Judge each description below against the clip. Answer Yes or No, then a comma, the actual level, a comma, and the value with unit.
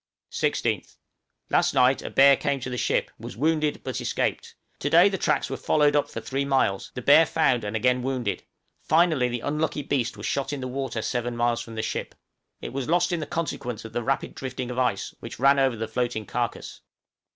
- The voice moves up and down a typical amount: Yes, average, 3.2 semitones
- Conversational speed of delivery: No, fast, 210 wpm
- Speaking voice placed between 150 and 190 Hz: No, low, 130 Hz